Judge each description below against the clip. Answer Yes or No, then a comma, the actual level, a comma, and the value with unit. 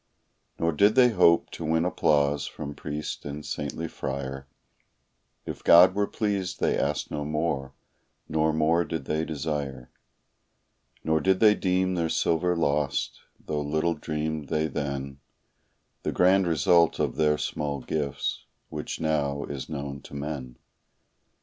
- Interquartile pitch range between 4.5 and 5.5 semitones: No, average, 2.8 semitones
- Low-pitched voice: Yes, very low, 75 Hz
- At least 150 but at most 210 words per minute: No, average, 140 wpm